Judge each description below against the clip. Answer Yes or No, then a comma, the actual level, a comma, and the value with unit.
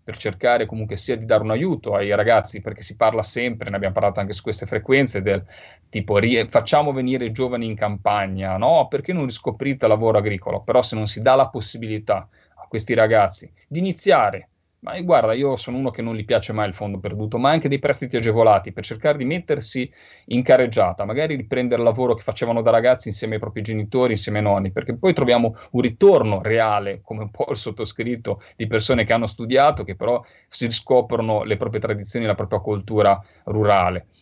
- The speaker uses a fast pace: Yes, fast, 200 wpm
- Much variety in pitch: No, average, 3.3 semitones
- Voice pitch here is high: No, low, 115 Hz